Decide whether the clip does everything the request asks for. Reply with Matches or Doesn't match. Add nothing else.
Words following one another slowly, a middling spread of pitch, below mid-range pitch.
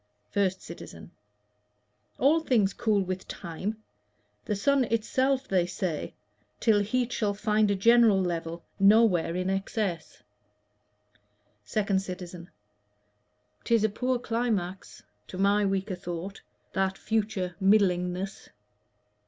Doesn't match